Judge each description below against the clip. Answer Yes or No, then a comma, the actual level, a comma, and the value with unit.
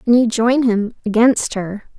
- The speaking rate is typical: Yes, average, 180 wpm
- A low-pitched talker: No, high, 225 Hz